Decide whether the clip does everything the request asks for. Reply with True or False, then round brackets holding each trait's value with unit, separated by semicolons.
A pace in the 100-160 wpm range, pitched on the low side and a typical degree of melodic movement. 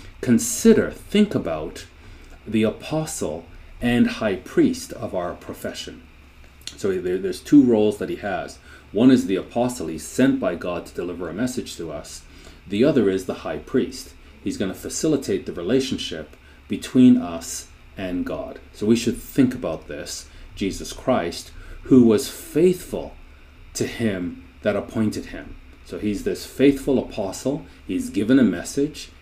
False (150 wpm; 100 Hz; 7.9 semitones)